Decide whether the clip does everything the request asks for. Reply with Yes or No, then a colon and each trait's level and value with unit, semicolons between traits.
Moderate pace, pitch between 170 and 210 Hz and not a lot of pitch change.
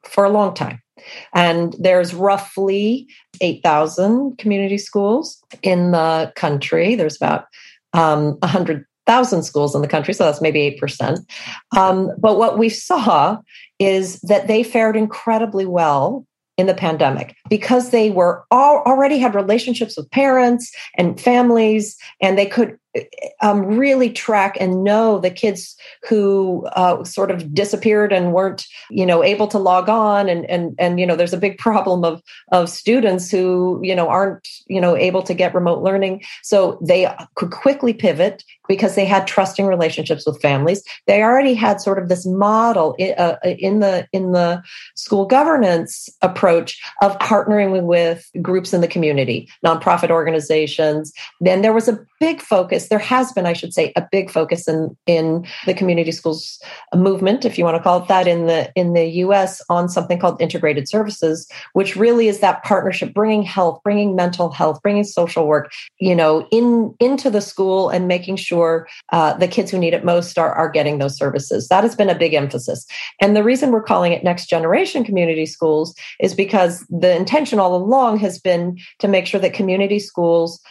No: average, 175 wpm; high, 190 Hz; average, 3.6 semitones